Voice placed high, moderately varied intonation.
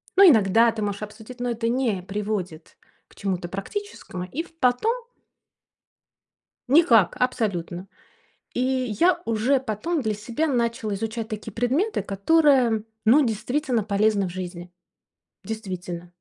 Yes: high, 220 Hz; average, 4.4 semitones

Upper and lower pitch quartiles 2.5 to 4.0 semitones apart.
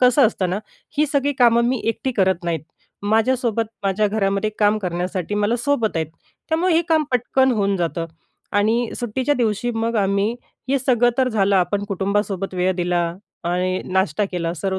No: average, 4.4 semitones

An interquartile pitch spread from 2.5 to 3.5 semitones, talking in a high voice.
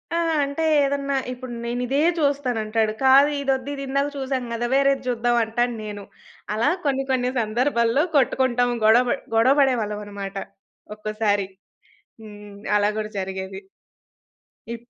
No: average, 4.1 semitones; high, 240 Hz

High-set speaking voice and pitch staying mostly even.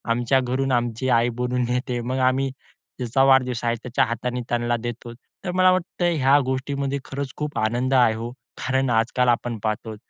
No: low, 125 Hz; narrow, 2.1 semitones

